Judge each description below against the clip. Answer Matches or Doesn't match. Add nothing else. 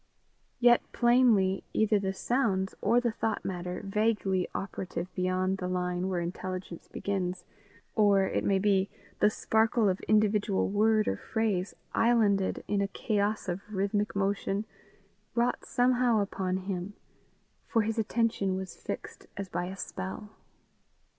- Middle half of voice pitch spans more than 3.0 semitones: Doesn't match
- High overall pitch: Matches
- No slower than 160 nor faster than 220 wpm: Doesn't match